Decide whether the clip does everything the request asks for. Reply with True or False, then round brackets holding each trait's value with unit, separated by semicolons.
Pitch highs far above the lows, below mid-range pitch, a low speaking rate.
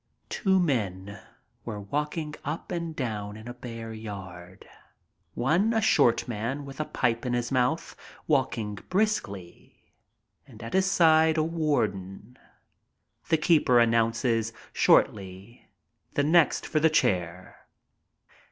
True (6.8 semitones; 120 Hz; 125 wpm)